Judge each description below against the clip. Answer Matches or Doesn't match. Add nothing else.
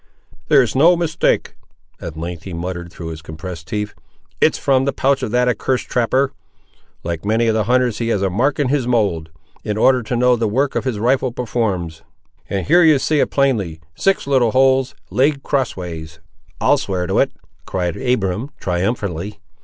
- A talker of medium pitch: Doesn't match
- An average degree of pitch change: Doesn't match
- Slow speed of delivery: Doesn't match